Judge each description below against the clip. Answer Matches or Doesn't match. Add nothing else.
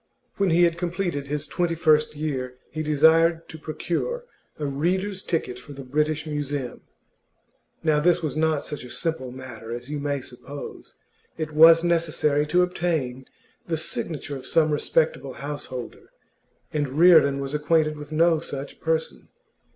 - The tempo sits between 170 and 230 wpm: Doesn't match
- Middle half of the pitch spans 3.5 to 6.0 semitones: Doesn't match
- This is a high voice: Doesn't match